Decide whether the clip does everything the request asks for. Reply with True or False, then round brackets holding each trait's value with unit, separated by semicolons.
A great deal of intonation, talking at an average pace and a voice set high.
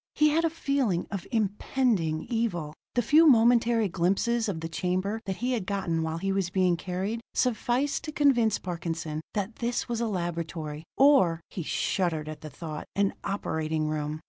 True (6.2 semitones; 170 wpm; 195 Hz)